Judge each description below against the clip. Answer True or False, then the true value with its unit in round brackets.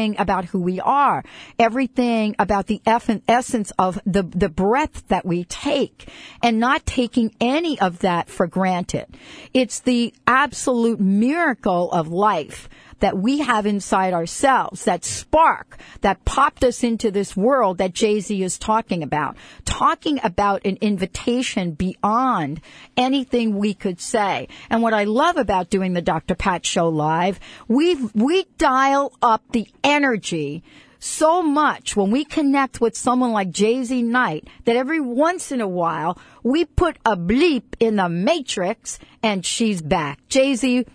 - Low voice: False (220 Hz)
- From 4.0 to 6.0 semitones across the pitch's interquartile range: True (5.2 semitones)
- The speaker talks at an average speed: True (150 wpm)